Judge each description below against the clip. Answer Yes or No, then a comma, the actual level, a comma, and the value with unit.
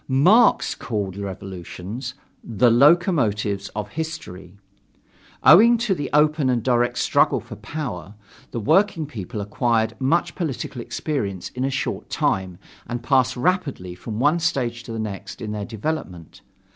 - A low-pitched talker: Yes, low, 120 Hz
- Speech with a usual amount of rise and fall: No, wide, 6.7 semitones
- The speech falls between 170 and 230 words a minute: No, average, 140 wpm